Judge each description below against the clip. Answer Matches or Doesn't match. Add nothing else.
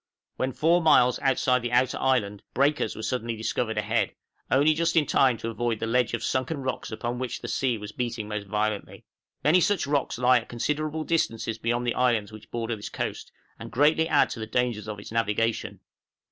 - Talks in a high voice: Doesn't match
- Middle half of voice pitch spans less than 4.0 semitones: Matches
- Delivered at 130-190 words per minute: Doesn't match